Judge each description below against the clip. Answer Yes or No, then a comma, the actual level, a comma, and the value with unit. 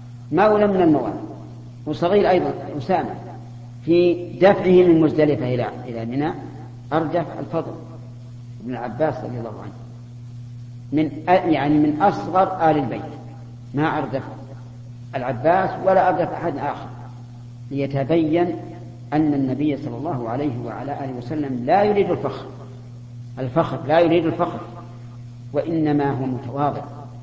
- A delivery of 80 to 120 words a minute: Yes, average, 115 wpm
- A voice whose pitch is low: Yes, low, 130 Hz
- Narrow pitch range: No, average, 4.6 semitones